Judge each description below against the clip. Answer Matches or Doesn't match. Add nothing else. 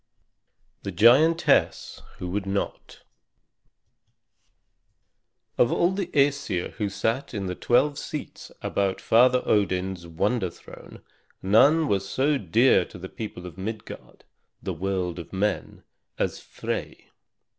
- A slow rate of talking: Matches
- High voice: Doesn't match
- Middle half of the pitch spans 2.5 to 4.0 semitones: Doesn't match